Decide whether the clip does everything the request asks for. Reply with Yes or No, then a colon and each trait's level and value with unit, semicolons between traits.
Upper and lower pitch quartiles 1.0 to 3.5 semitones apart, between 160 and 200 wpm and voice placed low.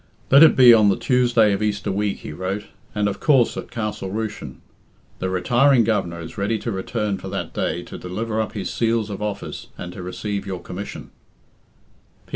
Yes: average, 3.0 semitones; average, 190 wpm; low, 105 Hz